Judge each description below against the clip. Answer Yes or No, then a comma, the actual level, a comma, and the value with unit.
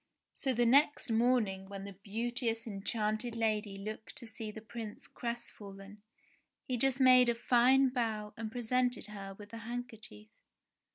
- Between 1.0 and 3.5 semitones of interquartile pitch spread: Yes, average, 2.7 semitones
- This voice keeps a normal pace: Yes, average, 150 wpm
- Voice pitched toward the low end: No, high, 225 Hz